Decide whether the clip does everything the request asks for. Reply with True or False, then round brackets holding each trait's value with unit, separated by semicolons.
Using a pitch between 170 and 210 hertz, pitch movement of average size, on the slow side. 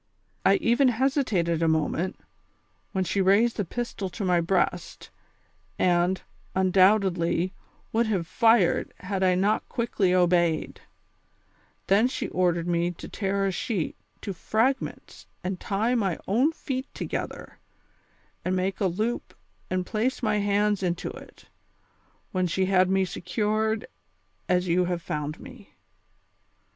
True (190 Hz; 3.4 semitones; 130 wpm)